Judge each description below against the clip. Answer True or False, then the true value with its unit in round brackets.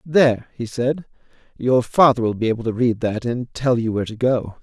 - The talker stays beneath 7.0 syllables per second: True (5.3 syllables/s)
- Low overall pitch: True (120 Hz)